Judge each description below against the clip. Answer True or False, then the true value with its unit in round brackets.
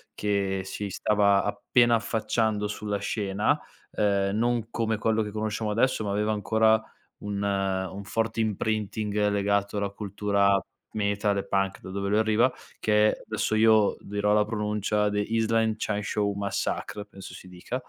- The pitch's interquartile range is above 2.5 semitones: False (1.5 semitones)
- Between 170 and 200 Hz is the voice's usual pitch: False (105 Hz)